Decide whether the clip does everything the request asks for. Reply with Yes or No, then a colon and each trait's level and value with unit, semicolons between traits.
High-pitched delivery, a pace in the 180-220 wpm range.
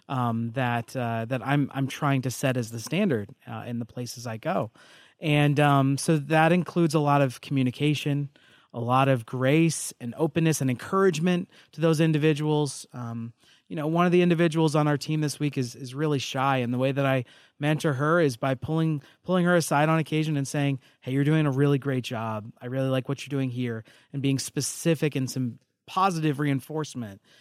No: medium, 140 Hz; average, 200 wpm